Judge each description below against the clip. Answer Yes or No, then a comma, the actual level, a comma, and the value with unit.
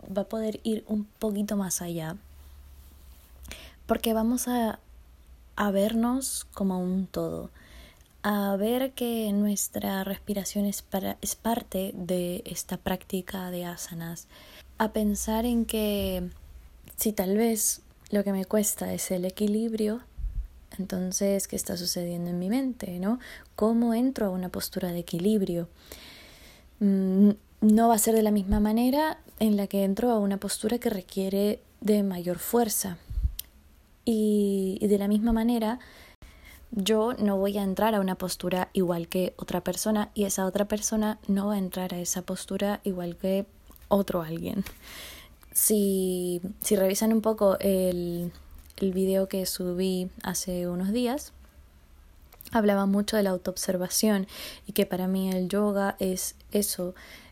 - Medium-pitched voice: No, high, 195 Hz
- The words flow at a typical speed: Yes, average, 145 wpm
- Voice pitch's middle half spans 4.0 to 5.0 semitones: No, average, 3.0 semitones